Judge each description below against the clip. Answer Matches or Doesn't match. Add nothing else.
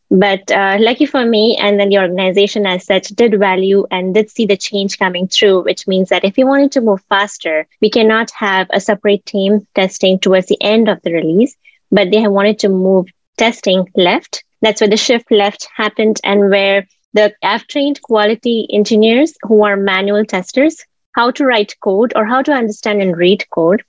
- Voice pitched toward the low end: Doesn't match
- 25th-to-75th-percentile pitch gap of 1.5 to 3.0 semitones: Matches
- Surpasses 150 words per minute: Matches